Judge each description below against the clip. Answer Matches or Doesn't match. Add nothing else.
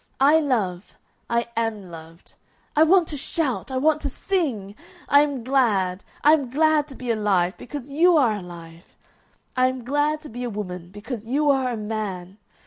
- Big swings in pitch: Matches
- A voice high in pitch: Matches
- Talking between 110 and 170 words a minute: Doesn't match